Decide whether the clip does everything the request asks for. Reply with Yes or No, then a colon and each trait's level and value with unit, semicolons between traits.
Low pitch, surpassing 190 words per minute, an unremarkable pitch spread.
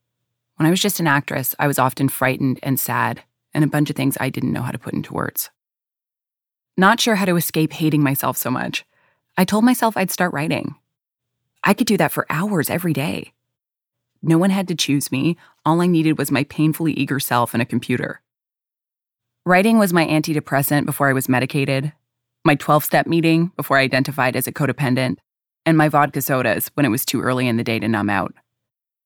No: medium, 145 Hz; average, 200 wpm; average, 4.0 semitones